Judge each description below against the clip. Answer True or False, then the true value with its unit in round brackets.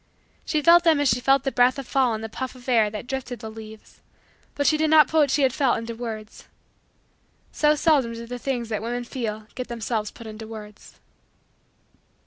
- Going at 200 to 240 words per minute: True (205 wpm)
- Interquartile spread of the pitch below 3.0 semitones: False (3.6 semitones)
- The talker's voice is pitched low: False (245 Hz)